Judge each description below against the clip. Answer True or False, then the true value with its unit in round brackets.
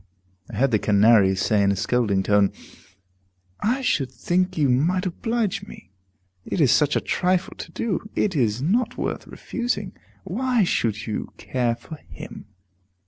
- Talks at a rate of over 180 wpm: False (155 wpm)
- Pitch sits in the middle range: True (145 Hz)